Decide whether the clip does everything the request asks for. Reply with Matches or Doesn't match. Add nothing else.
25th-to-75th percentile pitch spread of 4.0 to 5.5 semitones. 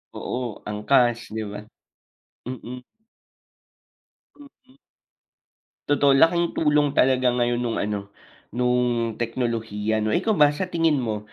Matches